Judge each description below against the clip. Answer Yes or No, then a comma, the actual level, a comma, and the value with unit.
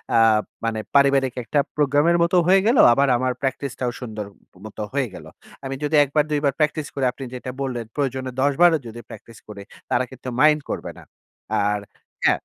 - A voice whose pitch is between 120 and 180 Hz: Yes, low, 135 Hz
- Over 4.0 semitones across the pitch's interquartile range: No, average, 3.0 semitones